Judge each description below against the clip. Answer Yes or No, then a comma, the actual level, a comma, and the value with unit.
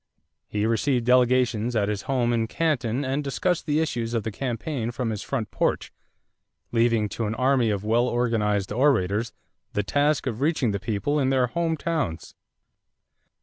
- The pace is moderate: Yes, average, 165 wpm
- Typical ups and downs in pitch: Yes, average, 3.8 semitones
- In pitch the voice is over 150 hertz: No, low, 120 Hz